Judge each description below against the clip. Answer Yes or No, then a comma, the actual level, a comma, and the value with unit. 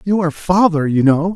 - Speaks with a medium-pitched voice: Yes, medium, 170 Hz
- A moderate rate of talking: No, fast, 220 wpm